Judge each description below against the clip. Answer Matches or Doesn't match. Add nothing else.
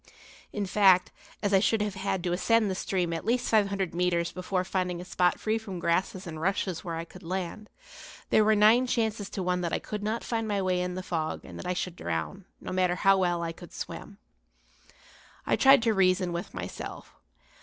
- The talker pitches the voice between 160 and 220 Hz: Matches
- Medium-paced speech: Doesn't match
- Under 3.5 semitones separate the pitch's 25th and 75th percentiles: Matches